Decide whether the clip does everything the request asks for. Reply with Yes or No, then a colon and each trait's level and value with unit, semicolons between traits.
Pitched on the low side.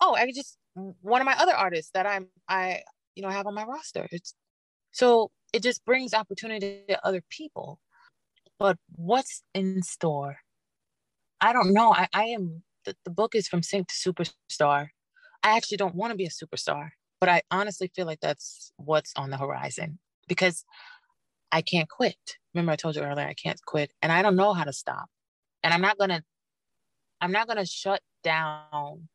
No: medium, 185 Hz